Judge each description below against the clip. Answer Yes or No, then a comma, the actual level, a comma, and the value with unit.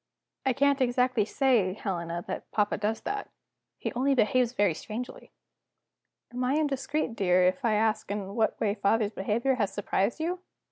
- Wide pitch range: No, average, 4.3 semitones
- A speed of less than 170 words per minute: Yes, average, 160 wpm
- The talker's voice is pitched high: Yes, high, 225 Hz